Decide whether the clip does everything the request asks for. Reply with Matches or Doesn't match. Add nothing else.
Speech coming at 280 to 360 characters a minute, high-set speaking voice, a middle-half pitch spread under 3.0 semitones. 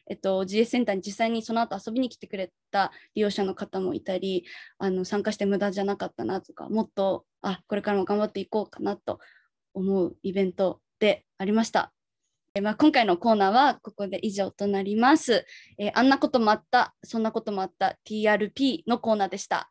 Doesn't match